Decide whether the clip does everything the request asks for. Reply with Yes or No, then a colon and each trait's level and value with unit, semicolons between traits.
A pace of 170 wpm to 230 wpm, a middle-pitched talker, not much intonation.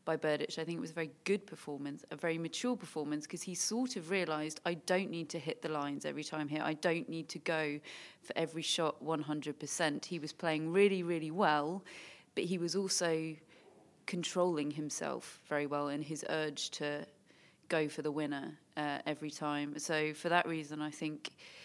Yes: average, 190 wpm; medium, 160 Hz; narrow, 2.3 semitones